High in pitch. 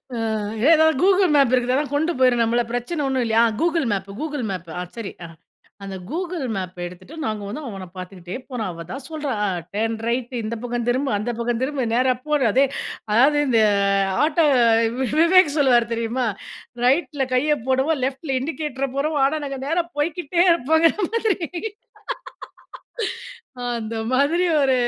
Yes: very high, 265 Hz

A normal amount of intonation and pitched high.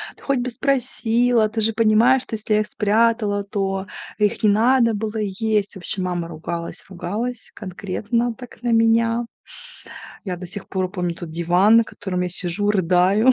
Yes: average, 3.6 semitones; high, 210 Hz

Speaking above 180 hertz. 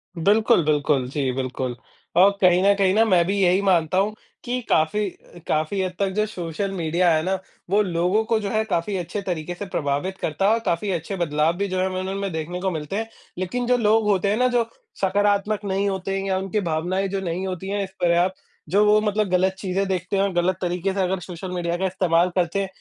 Yes: high, 190 Hz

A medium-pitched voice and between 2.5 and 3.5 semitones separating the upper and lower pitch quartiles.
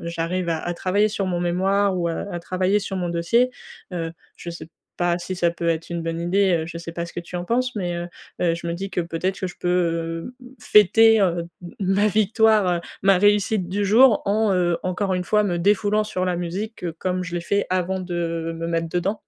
Yes: medium, 180 Hz; average, 2.9 semitones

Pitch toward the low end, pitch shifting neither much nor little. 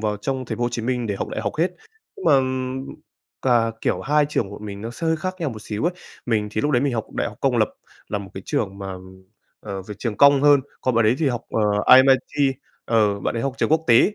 Yes: low, 120 Hz; average, 5.0 semitones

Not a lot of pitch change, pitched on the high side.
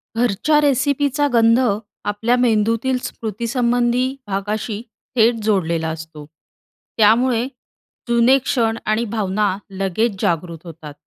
No: average, 3.9 semitones; high, 225 Hz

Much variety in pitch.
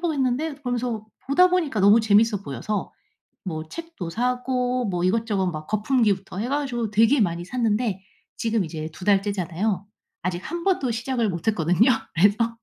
No: average, 4.8 semitones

